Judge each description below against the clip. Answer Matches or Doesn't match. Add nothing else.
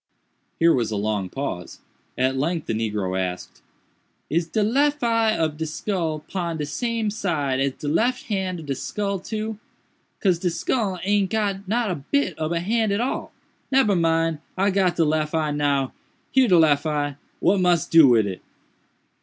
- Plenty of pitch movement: Matches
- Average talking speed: Matches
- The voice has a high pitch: Doesn't match